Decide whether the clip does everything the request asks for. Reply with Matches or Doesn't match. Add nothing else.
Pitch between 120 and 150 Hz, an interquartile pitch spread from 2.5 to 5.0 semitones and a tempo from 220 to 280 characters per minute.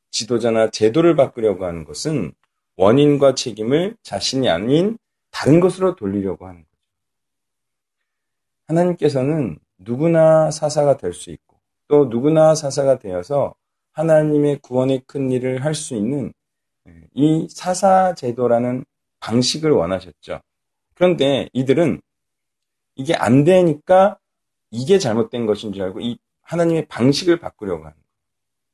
Doesn't match